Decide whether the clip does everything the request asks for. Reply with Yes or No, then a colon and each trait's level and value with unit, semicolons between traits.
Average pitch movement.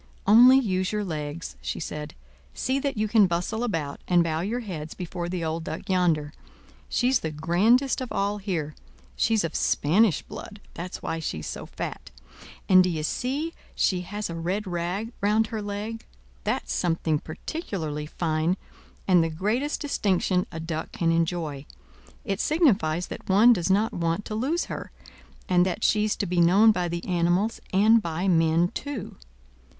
Yes: average, 4.6 semitones